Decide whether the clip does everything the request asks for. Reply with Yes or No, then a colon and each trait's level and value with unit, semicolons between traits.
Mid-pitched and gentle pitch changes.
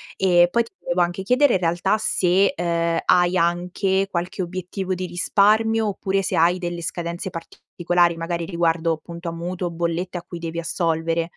Yes: medium, 175 Hz; narrow, 1.9 semitones